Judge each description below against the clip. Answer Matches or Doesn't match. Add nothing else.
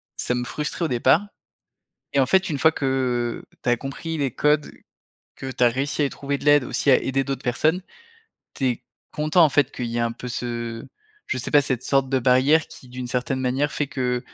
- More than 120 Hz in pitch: Matches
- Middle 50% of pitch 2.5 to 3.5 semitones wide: Matches